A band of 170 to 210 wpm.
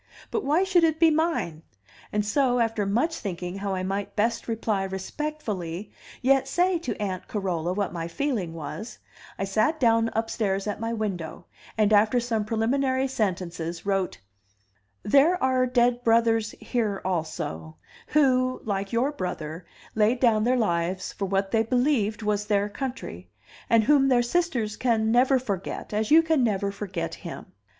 No: average, 160 wpm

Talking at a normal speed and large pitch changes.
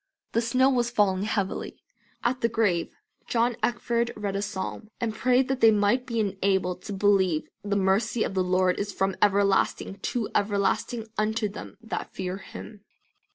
No: average, 165 wpm; average, 3.1 semitones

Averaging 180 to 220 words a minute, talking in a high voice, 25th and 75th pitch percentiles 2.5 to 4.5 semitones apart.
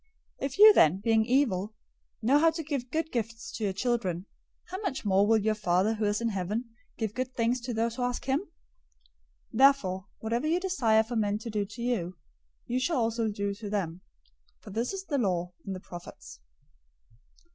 Yes: average, 200 wpm; high, 225 Hz; average, 4.1 semitones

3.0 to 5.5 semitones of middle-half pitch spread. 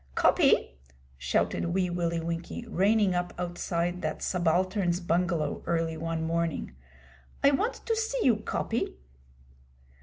No: narrow, 2.6 semitones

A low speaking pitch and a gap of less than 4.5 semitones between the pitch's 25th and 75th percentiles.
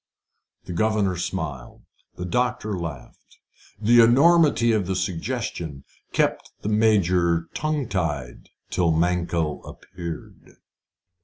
No: very low, 90 Hz; average, 5.1 semitones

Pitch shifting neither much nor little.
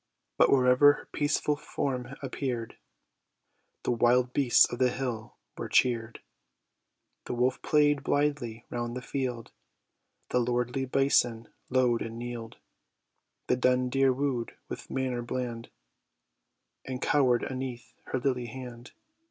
No: narrow, 1.8 semitones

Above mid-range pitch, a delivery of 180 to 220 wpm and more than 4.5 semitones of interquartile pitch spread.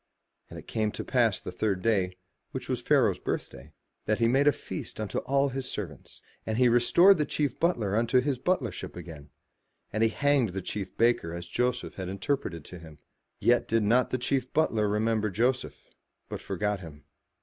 No: low, 110 Hz; average, 185 wpm; average, 5.2 semitones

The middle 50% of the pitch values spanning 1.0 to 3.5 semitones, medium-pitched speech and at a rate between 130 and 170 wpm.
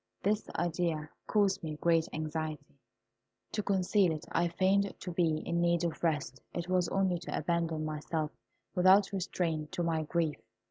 Yes: average, 2.7 semitones; medium, 170 Hz; average, 155 wpm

